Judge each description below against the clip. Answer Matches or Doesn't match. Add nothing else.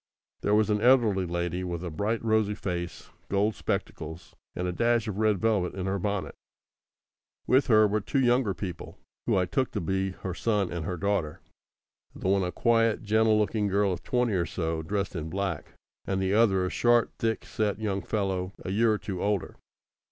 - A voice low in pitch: Matches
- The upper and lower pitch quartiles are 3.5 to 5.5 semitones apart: Doesn't match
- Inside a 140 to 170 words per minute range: Doesn't match